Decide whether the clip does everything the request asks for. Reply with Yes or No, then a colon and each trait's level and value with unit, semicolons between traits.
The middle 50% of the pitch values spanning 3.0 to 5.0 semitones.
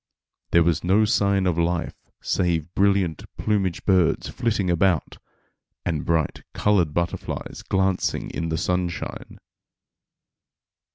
No: narrow, 2.6 semitones